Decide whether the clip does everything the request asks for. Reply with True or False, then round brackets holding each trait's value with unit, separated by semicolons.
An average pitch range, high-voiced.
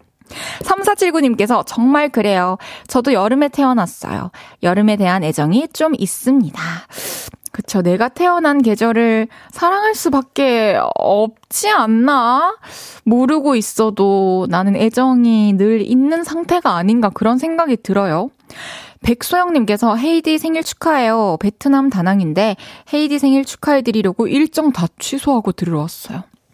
False (6.0 semitones; 240 Hz)